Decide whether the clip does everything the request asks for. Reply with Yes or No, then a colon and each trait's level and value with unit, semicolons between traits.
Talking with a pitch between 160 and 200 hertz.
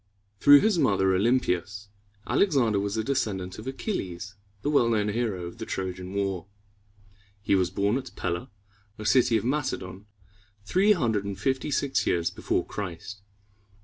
No: low, 105 Hz